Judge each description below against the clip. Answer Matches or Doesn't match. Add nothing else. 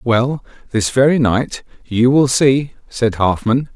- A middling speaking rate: Matches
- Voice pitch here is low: Matches